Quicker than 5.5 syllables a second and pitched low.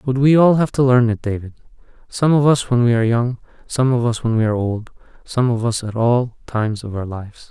Yes: 5.8 syllables/s; low, 120 Hz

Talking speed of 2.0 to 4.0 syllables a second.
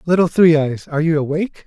No: 6.5 syllables/s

